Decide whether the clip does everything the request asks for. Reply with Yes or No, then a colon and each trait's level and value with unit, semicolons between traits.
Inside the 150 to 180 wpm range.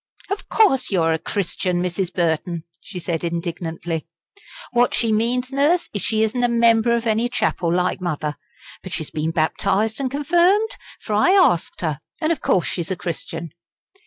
Yes: average, 170 wpm